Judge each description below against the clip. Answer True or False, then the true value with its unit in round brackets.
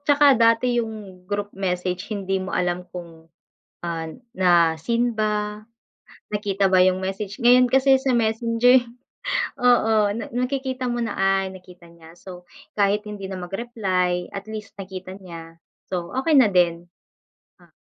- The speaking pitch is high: True (195 Hz)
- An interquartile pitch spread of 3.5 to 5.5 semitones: True (4.5 semitones)